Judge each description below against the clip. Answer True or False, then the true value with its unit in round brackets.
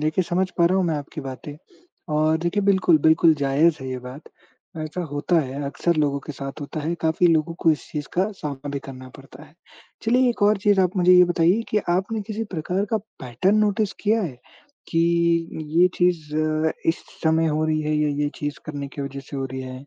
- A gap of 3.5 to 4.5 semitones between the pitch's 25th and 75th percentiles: True (3.9 semitones)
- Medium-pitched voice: True (160 Hz)